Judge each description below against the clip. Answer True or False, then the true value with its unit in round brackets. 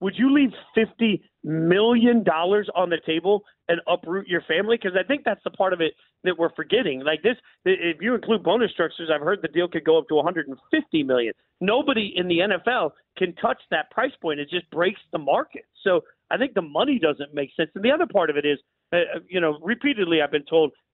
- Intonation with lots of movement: True (6.1 semitones)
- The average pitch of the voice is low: False (180 Hz)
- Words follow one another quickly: True (220 wpm)